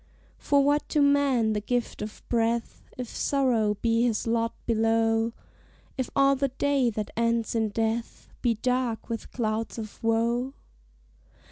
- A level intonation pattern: Yes, narrow, 2.3 semitones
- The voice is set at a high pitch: Yes, high, 230 Hz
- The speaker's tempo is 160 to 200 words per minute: No, average, 145 wpm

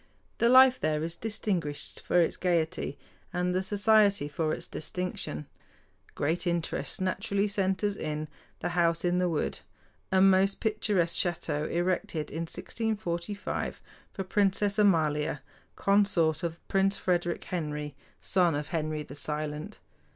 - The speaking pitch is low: No, medium, 175 Hz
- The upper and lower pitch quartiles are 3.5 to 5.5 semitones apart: Yes, average, 4.1 semitones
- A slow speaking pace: Yes, slow, 130 wpm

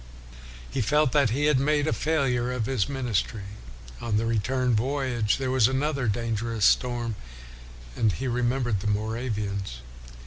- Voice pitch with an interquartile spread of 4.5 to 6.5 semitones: No, average, 3.4 semitones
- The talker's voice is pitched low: Yes, low, 120 Hz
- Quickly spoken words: No, average, 145 wpm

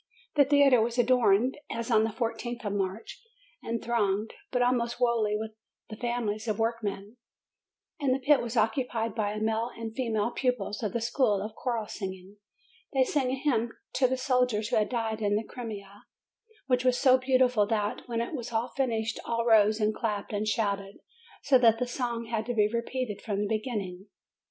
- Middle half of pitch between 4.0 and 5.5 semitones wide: No, average, 2.8 semitones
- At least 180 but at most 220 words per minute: Yes, average, 185 wpm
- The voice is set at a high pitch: Yes, high, 230 Hz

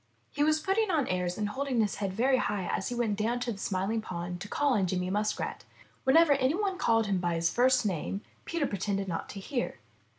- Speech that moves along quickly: Yes, fast, 225 wpm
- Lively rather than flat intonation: Yes, wide, 5.9 semitones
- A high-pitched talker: Yes, high, 215 Hz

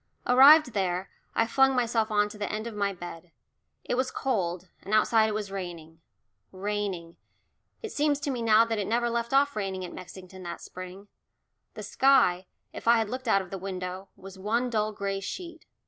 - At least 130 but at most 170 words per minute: No, average, 195 wpm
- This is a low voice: No, high, 210 Hz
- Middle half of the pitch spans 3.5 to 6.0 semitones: Yes, average, 4.1 semitones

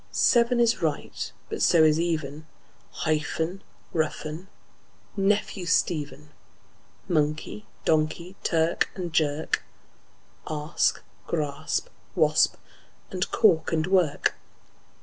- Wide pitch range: No, average, 3.1 semitones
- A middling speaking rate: No, slow, 90 wpm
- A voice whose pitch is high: No, medium, 160 Hz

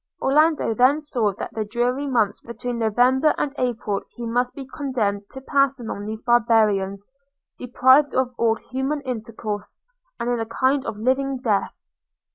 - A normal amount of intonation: Yes, average, 3.2 semitones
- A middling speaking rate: Yes, average, 155 wpm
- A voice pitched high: Yes, high, 245 Hz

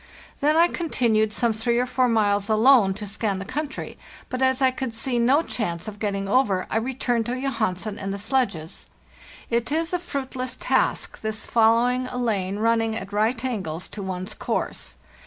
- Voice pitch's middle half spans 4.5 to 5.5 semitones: No, average, 3.8 semitones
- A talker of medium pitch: No, high, 230 Hz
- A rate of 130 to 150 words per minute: No, average, 190 wpm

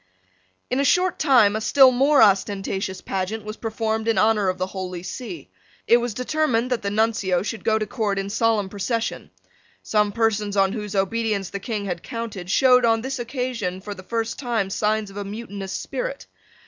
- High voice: Yes, high, 220 Hz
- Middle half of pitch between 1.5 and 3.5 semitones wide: Yes, average, 3.0 semitones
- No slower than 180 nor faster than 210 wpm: Yes, average, 185 wpm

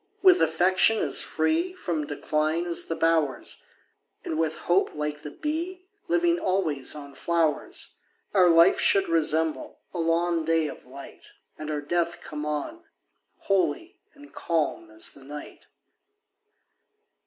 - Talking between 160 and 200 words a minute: No, slow, 135 wpm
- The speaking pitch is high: No, medium, 165 Hz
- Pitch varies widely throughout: Yes, wide, 5.7 semitones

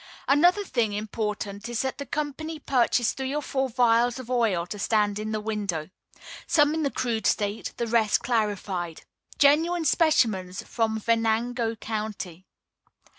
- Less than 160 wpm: Yes, average, 145 wpm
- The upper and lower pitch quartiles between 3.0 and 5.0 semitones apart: Yes, average, 4.1 semitones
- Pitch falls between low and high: No, high, 230 Hz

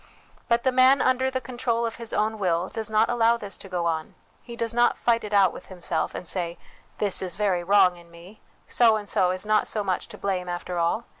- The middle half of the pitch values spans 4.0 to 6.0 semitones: Yes, average, 4.4 semitones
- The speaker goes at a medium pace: No, fast, 240 wpm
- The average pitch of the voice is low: No, high, 205 Hz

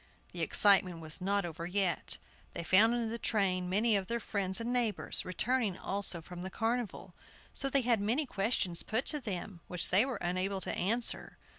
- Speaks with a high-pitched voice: Yes, high, 200 Hz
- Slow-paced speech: No, average, 185 wpm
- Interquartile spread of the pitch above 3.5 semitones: Yes, average, 4.1 semitones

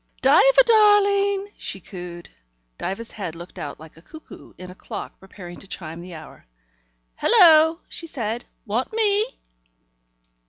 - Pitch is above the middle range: Yes, high, 230 Hz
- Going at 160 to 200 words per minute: No, slow, 135 wpm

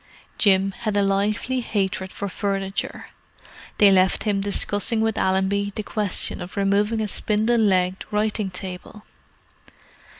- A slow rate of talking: Yes, slow, 130 wpm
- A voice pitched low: No, high, 200 Hz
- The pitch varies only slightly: Yes, narrow, 1.8 semitones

